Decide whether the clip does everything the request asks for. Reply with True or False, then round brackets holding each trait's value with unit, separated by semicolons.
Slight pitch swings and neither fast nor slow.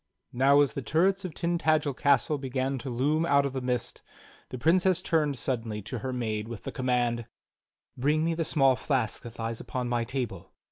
False (4.1 semitones; 190 wpm)